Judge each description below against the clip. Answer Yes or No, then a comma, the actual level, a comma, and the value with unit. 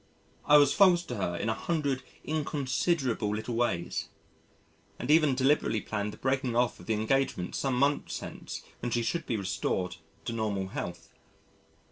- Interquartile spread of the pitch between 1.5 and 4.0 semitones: No, average, 4.9 semitones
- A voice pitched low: Yes, low, 125 Hz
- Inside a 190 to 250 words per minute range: No, average, 160 wpm